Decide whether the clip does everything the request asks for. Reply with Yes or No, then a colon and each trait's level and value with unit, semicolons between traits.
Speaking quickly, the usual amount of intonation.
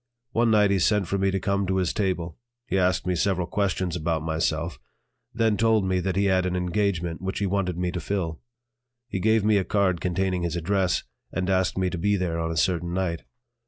No: fast, 220 wpm; narrow, 2.3 semitones